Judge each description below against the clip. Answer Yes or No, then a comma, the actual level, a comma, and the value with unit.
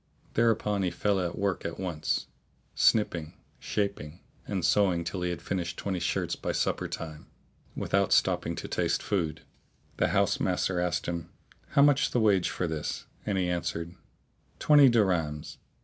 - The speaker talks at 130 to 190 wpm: Yes, average, 155 wpm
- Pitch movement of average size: Yes, average, 3.2 semitones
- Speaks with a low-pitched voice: Yes, very low, 90 Hz